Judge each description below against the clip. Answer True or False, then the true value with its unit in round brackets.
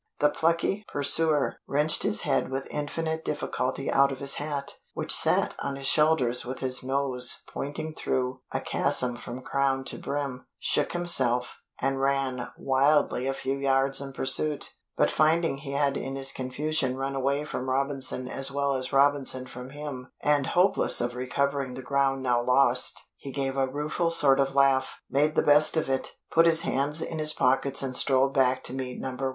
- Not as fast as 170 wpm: False (180 wpm)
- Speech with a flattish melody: True (1.9 semitones)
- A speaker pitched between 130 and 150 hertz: True (135 Hz)